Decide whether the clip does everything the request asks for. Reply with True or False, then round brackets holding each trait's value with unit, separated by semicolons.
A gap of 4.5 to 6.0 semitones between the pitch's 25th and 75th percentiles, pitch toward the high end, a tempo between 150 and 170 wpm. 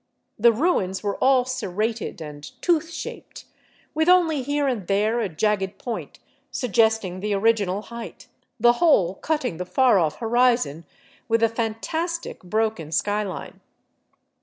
False (4.8 semitones; 225 Hz; 135 wpm)